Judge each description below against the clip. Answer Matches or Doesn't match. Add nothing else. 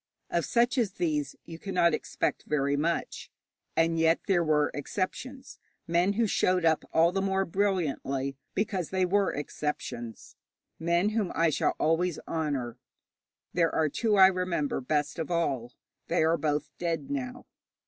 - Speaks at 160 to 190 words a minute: Doesn't match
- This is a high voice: Doesn't match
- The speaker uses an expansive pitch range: Doesn't match